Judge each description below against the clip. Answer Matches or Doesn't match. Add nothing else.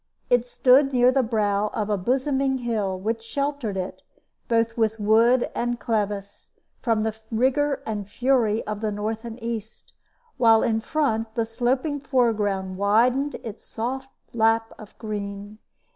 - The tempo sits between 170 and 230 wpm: Doesn't match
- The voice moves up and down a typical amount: Matches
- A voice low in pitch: Doesn't match